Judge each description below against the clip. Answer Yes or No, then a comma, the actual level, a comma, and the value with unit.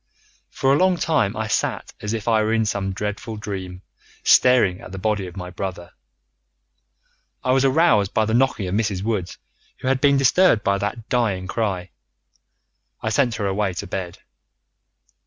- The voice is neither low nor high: No, low, 105 Hz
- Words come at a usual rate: Yes, average, 175 wpm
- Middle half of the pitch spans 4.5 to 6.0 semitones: No, average, 4.1 semitones